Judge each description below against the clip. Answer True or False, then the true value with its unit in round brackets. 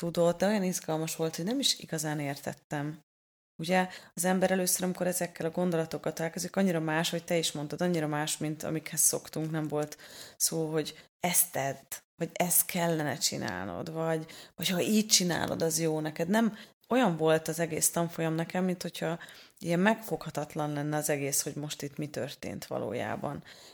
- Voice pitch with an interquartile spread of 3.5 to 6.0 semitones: False (2.6 semitones)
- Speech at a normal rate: False (170 wpm)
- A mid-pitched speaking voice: True (165 Hz)